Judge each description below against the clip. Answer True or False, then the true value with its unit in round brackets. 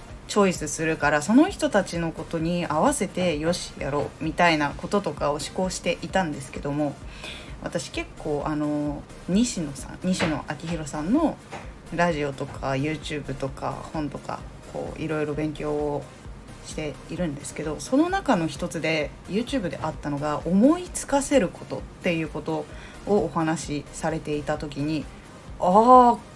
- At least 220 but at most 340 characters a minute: True (330 characters per minute)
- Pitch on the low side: False (160 Hz)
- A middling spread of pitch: True (3.6 semitones)